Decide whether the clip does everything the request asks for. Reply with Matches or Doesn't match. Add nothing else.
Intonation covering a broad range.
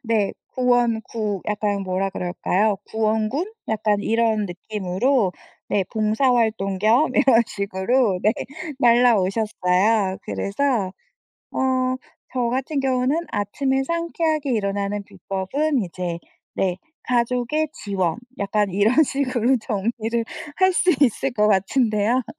Doesn't match